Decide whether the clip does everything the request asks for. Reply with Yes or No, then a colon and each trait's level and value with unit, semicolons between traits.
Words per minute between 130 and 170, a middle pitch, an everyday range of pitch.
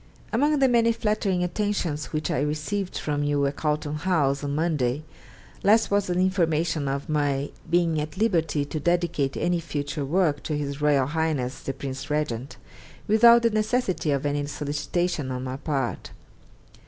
Yes: average, 160 wpm; medium, 155 Hz; average, 4.2 semitones